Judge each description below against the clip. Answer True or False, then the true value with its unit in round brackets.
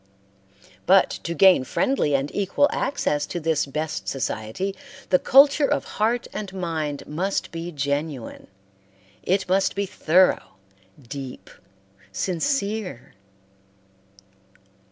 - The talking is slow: True (105 wpm)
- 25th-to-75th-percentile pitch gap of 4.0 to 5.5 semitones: True (5.2 semitones)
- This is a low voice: False (175 Hz)